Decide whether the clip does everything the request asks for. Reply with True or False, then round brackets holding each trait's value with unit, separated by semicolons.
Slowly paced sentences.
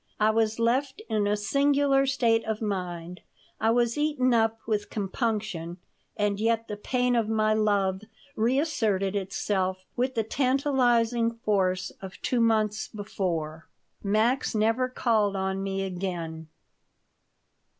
True (130 wpm)